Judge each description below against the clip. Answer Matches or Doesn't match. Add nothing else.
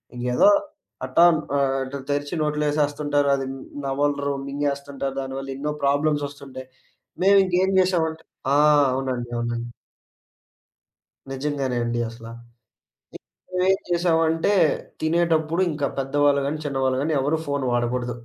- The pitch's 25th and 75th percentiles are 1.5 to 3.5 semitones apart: Matches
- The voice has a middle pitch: Matches